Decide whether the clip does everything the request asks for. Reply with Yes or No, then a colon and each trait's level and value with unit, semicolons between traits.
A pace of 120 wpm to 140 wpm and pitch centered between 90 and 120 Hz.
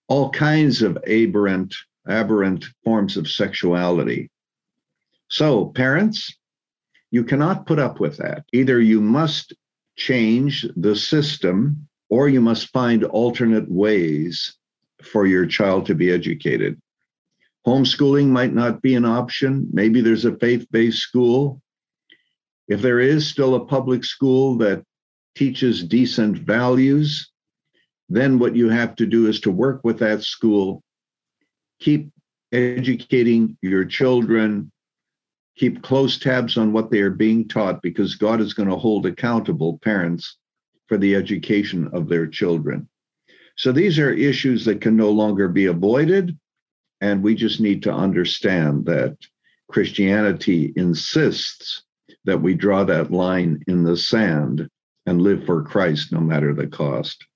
Yes: slow, 135 wpm; low, 115 Hz